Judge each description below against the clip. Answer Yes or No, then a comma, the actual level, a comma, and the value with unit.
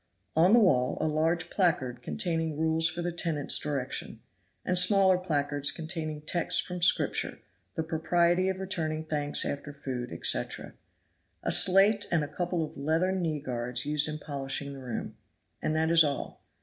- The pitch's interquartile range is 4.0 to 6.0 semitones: No, average, 3.3 semitones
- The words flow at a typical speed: Yes, average, 160 wpm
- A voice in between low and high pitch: Yes, medium, 160 Hz